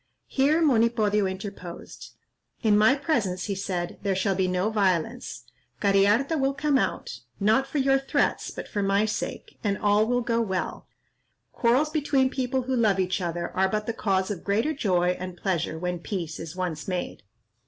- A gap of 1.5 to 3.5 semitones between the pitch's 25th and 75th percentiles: No, average, 5.0 semitones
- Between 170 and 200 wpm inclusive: Yes, average, 175 wpm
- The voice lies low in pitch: No, high, 205 Hz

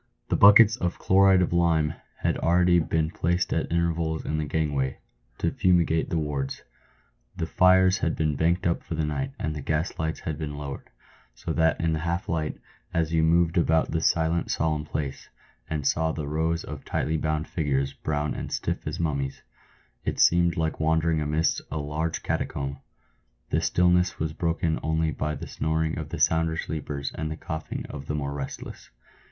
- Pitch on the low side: Yes, very low, 80 Hz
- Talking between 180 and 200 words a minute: Yes, average, 185 wpm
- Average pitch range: No, narrow, 1.8 semitones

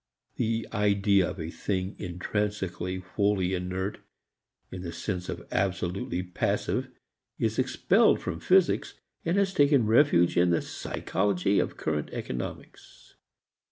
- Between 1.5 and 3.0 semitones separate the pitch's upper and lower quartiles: Yes, average, 2.7 semitones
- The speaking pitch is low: Yes, very low, 95 Hz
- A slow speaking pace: Yes, slow, 120 wpm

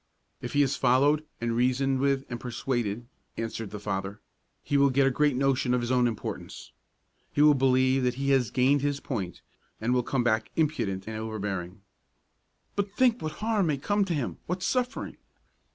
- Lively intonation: No, average, 3.7 semitones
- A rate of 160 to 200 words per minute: Yes, average, 185 wpm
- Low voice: Yes, low, 130 Hz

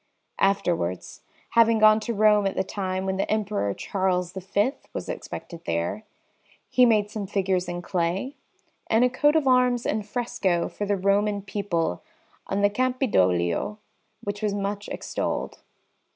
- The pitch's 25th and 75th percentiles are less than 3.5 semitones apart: Yes, narrow, 2.6 semitones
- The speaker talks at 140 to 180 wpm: Yes, average, 150 wpm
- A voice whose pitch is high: Yes, high, 200 Hz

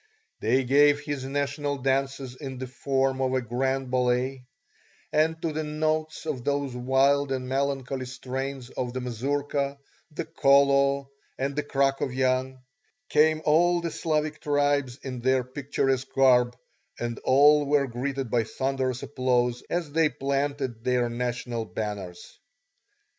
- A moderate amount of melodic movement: No, narrow, 2.1 semitones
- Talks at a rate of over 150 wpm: No, slow, 135 wpm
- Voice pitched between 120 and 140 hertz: Yes, low, 135 Hz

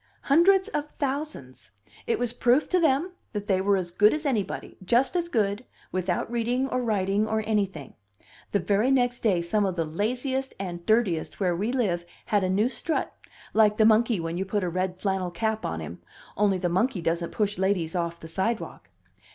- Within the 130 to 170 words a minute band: No, average, 190 wpm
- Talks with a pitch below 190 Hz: No, high, 205 Hz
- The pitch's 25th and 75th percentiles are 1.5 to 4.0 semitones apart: No, average, 5.1 semitones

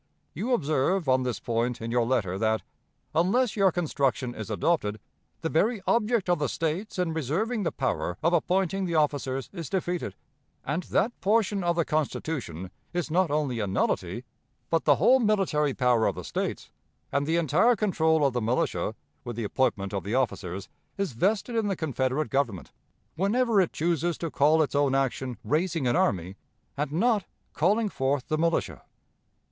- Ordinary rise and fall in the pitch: No, wide, 6.5 semitones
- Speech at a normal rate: Yes, average, 175 wpm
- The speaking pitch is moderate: Yes, medium, 155 Hz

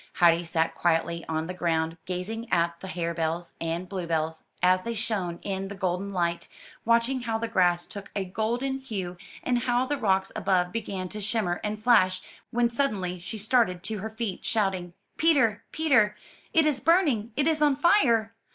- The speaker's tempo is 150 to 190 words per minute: Yes, average, 180 wpm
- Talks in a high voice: Yes, high, 200 Hz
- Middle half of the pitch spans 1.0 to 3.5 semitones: No, average, 4.8 semitones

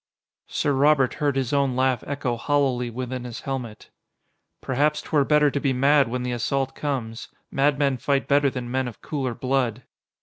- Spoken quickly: No, average, 170 wpm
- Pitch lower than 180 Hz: Yes, low, 135 Hz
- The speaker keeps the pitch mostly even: Yes, narrow, 2.3 semitones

